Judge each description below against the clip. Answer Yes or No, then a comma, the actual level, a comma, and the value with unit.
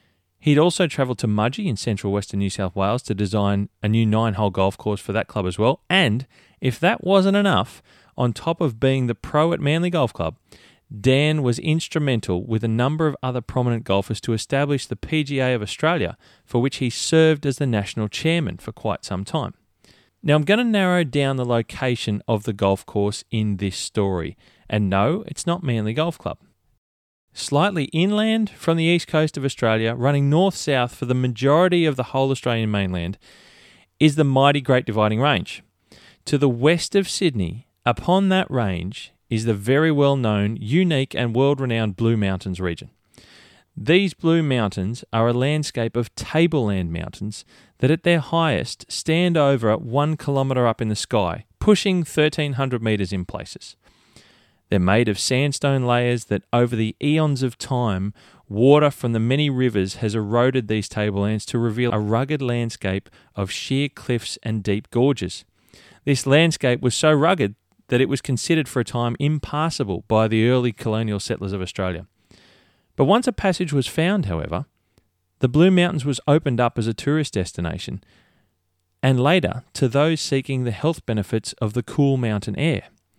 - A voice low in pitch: Yes, low, 125 Hz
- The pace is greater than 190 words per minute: No, average, 175 wpm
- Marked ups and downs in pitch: Yes, wide, 5.7 semitones